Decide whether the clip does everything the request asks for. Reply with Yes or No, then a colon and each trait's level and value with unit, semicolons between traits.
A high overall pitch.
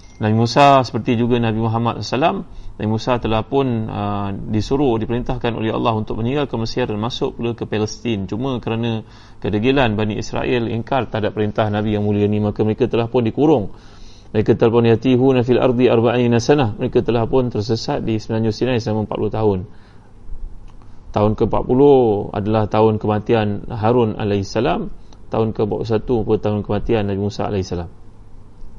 No: low, 110 Hz